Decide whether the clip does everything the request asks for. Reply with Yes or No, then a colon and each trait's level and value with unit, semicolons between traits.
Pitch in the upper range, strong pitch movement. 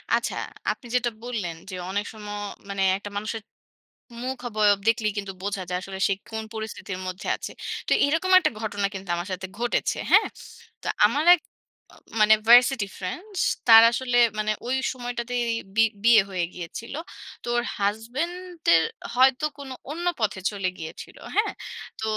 No: high, 220 Hz; average, 3.9 semitones